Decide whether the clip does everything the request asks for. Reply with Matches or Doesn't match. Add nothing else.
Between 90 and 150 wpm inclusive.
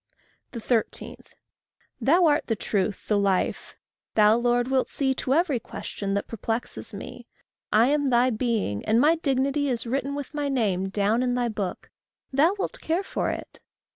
Doesn't match